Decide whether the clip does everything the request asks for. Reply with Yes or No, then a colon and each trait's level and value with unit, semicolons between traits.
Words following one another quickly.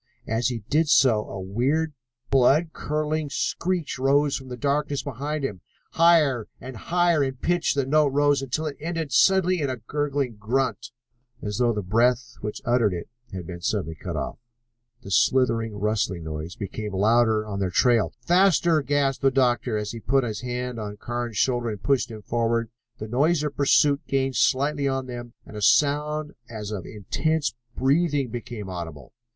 No: average, 175 wpm